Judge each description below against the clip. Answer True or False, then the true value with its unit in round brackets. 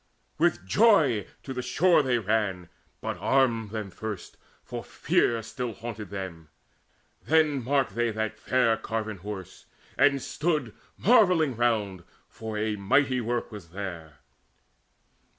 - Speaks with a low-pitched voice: True (115 Hz)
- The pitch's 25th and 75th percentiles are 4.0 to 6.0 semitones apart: True (4.7 semitones)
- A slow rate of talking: True (130 wpm)